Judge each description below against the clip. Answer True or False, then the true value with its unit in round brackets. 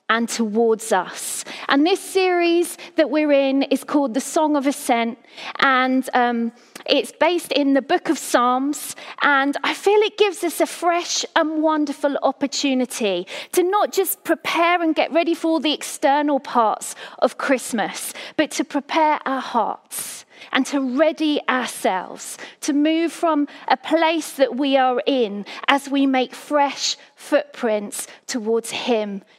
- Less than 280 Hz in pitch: False (285 Hz)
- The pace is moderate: True (150 wpm)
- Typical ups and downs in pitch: True (3.7 semitones)